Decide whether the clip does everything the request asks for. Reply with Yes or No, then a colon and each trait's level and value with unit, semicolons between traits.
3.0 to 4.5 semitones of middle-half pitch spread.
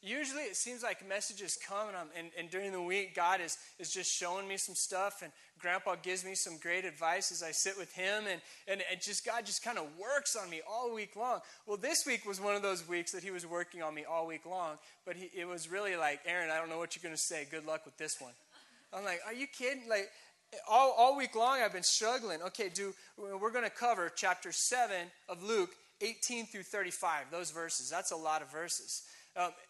Yes: average, 3.7 semitones